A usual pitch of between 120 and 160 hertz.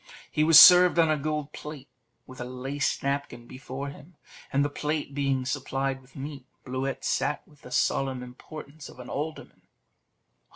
Yes: medium, 140 Hz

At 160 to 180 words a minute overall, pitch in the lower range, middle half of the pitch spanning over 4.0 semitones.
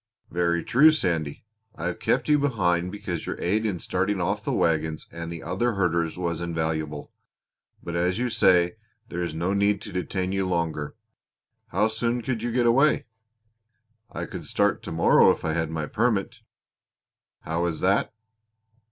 Yes: average, 170 wpm; very low, 90 Hz; average, 4.5 semitones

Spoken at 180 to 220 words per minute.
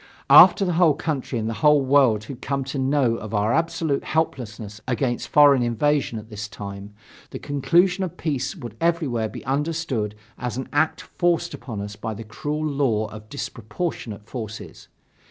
No: average, 170 wpm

